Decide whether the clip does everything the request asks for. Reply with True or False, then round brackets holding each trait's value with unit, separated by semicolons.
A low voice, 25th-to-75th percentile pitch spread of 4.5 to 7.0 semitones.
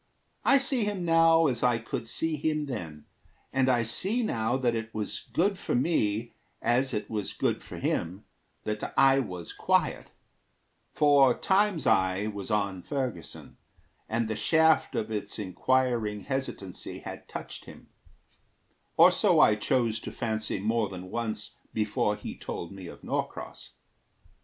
True (115 Hz; 5.0 semitones)